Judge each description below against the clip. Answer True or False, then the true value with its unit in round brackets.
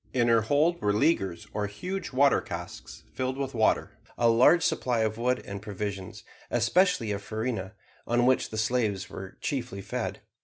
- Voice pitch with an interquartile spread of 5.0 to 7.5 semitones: False (3.9 semitones)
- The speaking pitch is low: True (115 Hz)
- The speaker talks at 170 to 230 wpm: False (160 wpm)